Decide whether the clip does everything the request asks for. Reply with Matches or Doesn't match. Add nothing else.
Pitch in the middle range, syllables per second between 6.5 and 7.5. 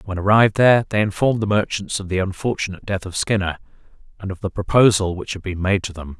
Doesn't match